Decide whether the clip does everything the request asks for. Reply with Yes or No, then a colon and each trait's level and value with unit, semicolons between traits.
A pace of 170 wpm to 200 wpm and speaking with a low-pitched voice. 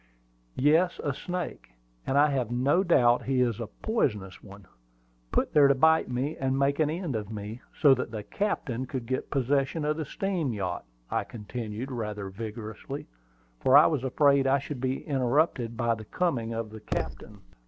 Yes: average, 180 wpm; low, 130 Hz